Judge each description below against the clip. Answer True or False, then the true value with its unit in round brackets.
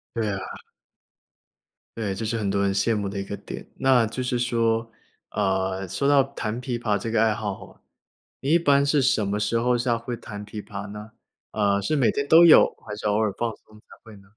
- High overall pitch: False (110 Hz)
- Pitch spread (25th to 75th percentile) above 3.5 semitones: False (3.2 semitones)